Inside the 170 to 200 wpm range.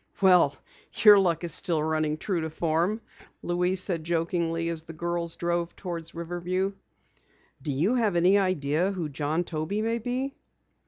No: average, 155 wpm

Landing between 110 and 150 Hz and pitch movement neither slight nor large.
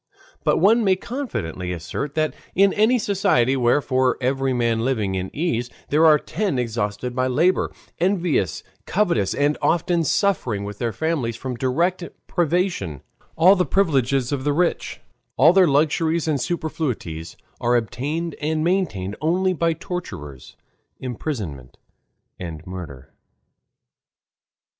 No: medium, 140 Hz; wide, 6.9 semitones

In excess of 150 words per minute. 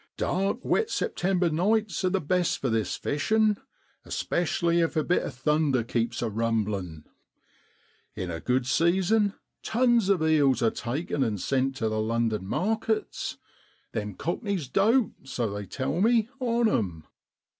No: average, 145 wpm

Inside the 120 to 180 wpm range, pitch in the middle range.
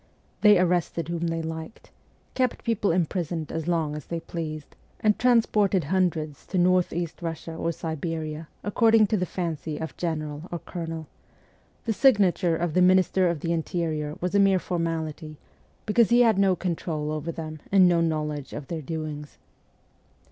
Yes: average, 160 wpm; medium, 170 Hz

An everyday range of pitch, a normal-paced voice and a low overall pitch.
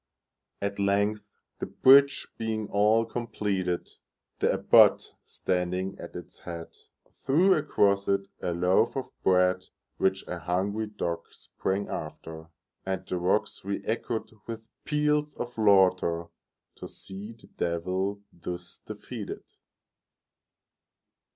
No: average, 3.5 semitones; slow, 100 wpm; low, 100 Hz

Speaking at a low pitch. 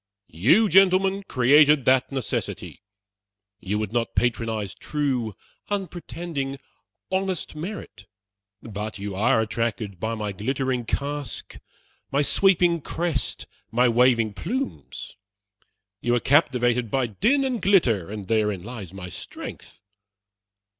Yes: low, 125 Hz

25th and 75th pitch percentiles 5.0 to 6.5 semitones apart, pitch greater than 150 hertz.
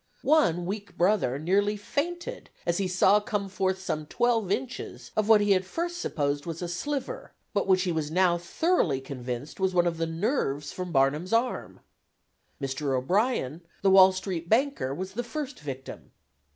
Yes: average, 5.3 semitones; medium, 185 Hz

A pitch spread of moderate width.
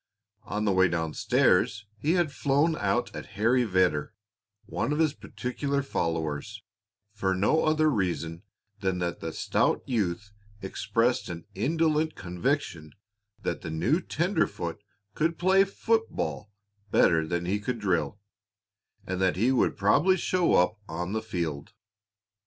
No: wide, 8.5 semitones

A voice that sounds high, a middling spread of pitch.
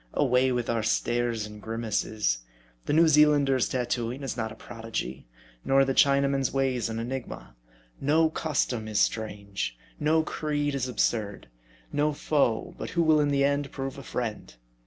No: low, 130 Hz; average, 4.1 semitones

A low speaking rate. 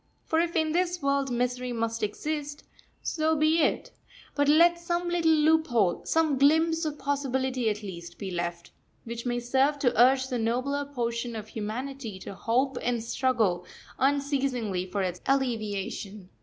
No: average, 155 wpm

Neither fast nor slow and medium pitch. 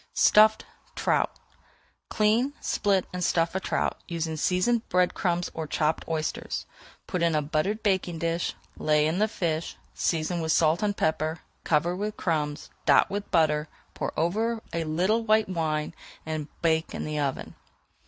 Yes: average, 155 wpm; medium, 170 Hz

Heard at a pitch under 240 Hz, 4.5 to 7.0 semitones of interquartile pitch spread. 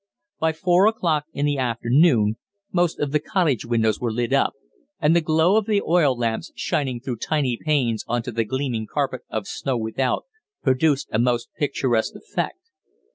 Yes: low, 135 Hz; average, 5.0 semitones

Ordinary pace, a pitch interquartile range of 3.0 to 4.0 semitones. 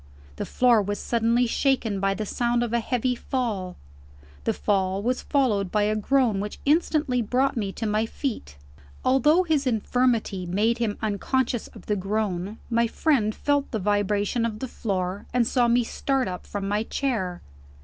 Yes: average, 170 wpm; average, 3.6 semitones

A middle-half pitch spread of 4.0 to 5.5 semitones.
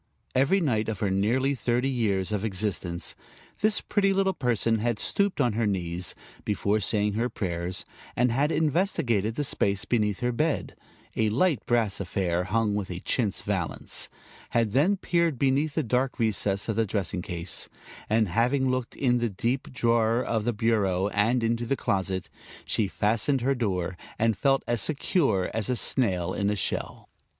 Yes: average, 4.5 semitones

